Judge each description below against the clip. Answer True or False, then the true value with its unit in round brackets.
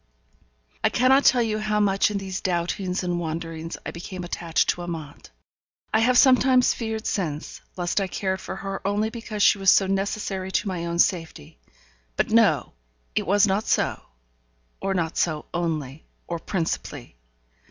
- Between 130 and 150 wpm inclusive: False (165 wpm)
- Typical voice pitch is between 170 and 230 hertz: True (190 Hz)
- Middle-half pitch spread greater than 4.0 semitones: False (3.7 semitones)